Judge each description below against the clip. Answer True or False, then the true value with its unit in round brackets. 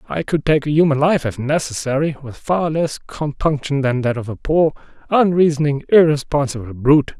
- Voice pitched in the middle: True (145 Hz)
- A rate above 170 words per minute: False (165 wpm)